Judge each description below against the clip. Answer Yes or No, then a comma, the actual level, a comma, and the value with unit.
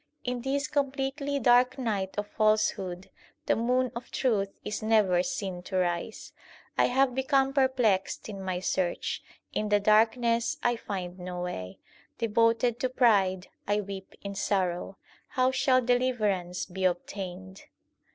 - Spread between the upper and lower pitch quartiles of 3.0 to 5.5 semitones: Yes, average, 5.0 semitones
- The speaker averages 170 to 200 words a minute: No, average, 140 wpm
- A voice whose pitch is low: No, high, 215 Hz